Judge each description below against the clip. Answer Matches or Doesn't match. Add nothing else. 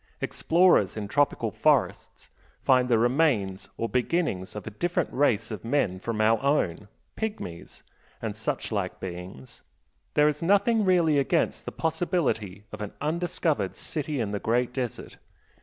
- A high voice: Doesn't match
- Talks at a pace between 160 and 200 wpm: Doesn't match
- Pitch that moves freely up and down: Matches